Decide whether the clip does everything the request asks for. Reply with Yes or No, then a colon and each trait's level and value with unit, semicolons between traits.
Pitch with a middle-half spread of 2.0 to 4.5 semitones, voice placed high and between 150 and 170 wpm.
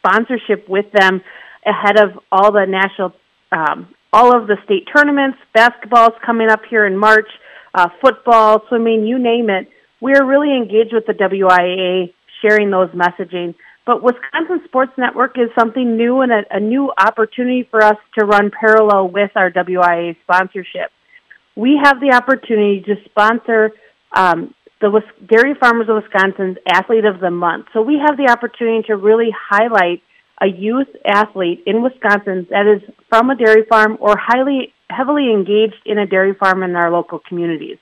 Yes: average, 3.6 semitones; high, 215 Hz; average, 165 wpm